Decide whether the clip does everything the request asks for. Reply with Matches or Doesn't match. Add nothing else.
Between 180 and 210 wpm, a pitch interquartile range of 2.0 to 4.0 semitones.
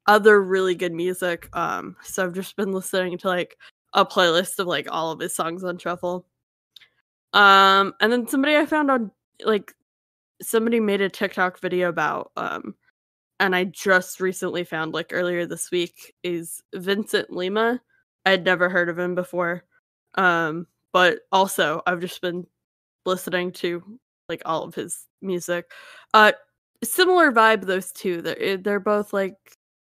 Doesn't match